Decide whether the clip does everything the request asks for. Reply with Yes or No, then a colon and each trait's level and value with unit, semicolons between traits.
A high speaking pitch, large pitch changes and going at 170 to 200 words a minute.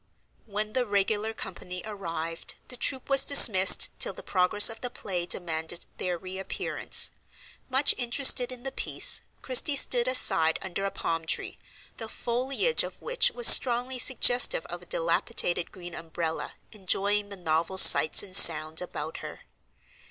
No: high, 205 Hz; wide, 6.1 semitones; average, 150 wpm